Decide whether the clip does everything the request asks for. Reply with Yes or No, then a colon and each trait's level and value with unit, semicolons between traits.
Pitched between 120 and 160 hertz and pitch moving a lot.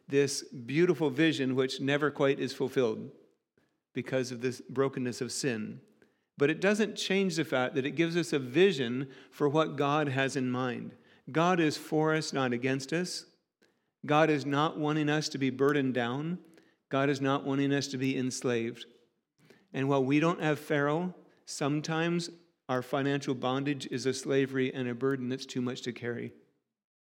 No: medium, 140 Hz; average, 2.9 semitones